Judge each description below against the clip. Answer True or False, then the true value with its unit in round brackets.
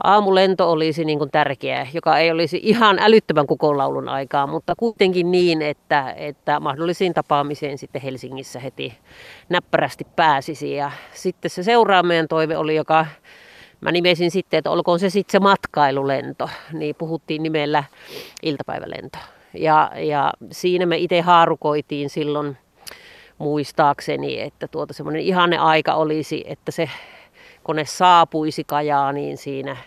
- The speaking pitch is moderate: True (160 Hz)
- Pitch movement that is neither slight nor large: True (3.0 semitones)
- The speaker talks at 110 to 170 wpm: True (135 wpm)